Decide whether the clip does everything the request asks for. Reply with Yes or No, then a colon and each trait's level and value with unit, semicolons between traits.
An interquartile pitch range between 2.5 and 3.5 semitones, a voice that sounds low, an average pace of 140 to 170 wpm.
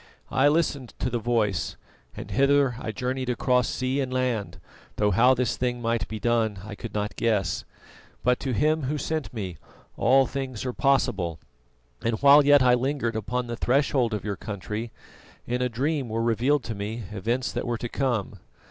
No: average, 3.2 semitones; low, 120 Hz; average, 185 wpm